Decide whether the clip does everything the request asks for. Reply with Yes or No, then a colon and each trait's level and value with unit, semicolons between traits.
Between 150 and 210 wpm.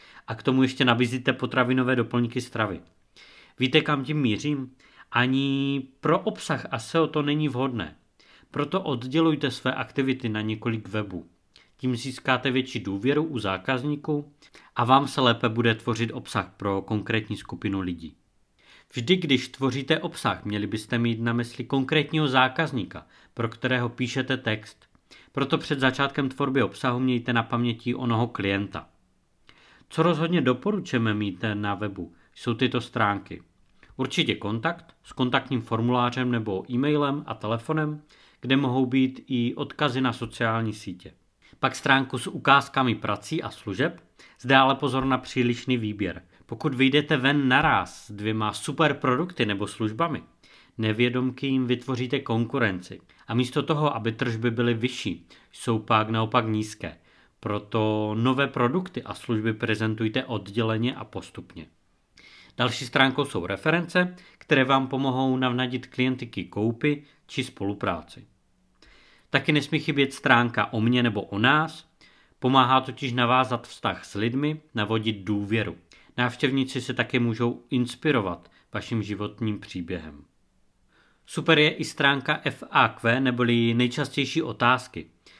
No: average, 130 wpm